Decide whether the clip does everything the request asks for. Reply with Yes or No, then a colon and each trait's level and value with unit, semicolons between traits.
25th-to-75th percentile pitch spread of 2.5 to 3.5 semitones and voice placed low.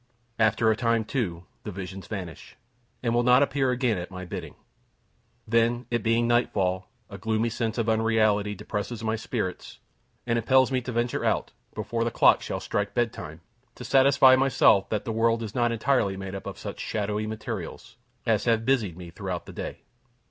Yes: average, 2.8 semitones; low, 110 Hz